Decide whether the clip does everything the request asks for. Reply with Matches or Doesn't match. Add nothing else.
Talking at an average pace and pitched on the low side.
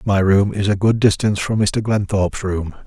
Doesn't match